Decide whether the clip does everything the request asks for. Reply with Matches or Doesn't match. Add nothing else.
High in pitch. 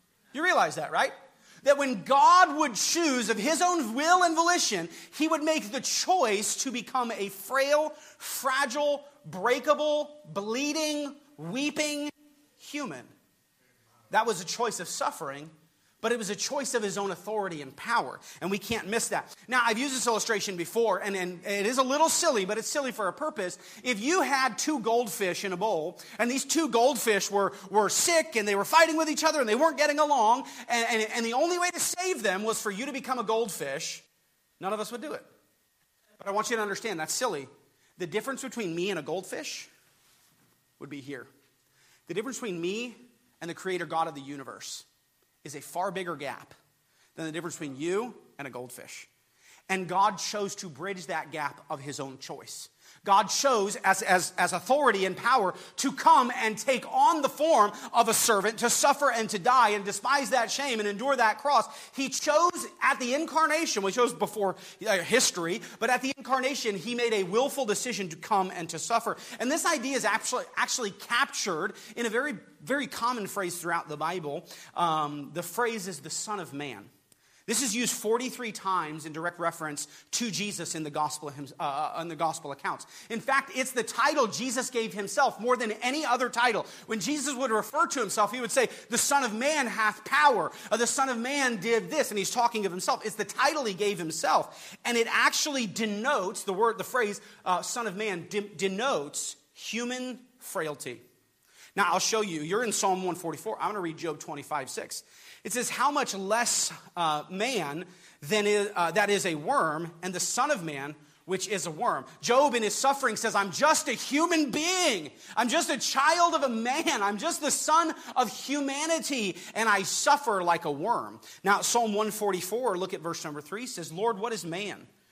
Matches